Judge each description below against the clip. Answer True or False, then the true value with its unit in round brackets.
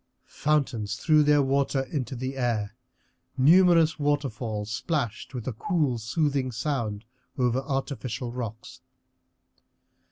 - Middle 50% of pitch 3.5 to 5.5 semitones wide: True (4.0 semitones)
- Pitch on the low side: True (130 Hz)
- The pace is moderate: False (105 wpm)